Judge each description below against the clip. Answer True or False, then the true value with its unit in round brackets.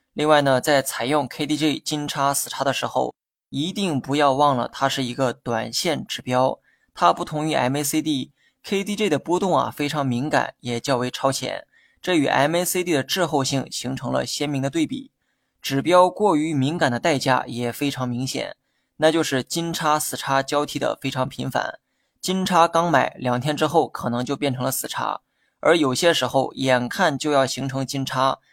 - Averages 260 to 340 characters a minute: True (270 characters per minute)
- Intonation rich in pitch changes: False (3.0 semitones)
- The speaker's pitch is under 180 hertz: True (140 Hz)